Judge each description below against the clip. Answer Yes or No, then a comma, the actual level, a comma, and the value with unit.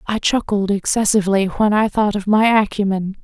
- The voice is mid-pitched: No, high, 205 Hz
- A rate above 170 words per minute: No, average, 165 wpm